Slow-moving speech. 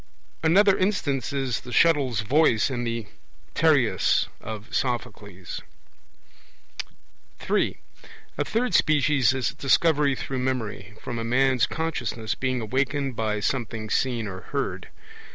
Yes: slow, 115 wpm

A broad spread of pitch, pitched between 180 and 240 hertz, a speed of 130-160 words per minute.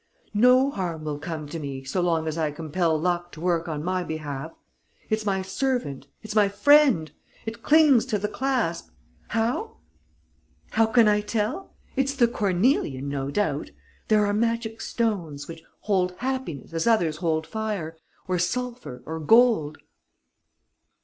Yes: wide, 6.3 semitones; high, 190 Hz; average, 150 wpm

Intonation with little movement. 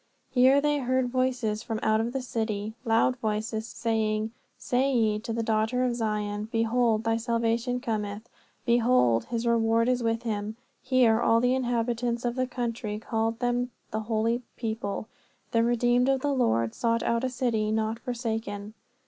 Yes: narrow, 2.0 semitones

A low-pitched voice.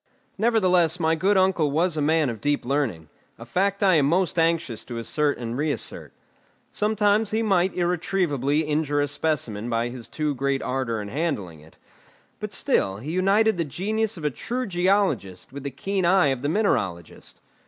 No: medium, 155 Hz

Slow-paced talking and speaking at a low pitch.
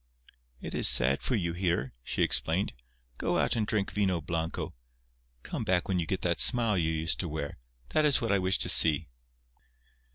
No: average, 190 wpm; very low, 90 Hz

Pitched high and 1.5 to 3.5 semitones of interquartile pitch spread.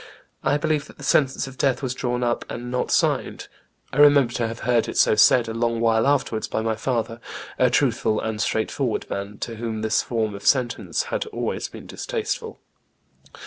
No: low, 120 Hz; average, 3.2 semitones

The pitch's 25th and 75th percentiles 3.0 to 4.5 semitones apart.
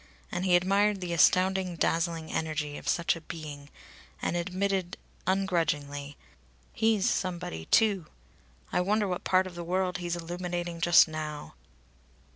No: narrow, 2.5 semitones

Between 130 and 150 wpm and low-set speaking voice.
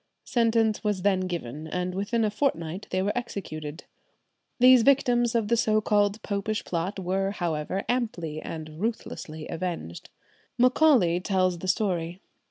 No: average, 140 wpm; high, 195 Hz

